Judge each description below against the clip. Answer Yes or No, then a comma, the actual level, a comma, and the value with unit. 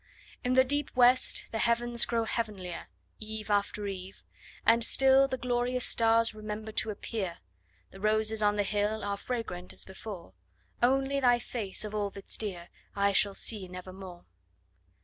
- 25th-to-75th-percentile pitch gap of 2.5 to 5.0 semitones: Yes, average, 3.2 semitones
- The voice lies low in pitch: No, high, 215 Hz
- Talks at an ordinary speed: Yes, average, 155 wpm